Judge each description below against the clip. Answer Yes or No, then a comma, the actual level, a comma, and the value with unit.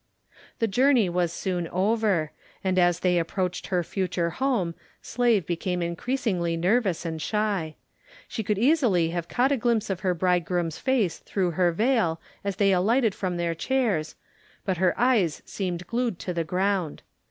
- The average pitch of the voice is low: No, medium, 185 Hz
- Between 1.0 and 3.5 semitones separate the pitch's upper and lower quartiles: No, average, 4.4 semitones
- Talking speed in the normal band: Yes, average, 160 wpm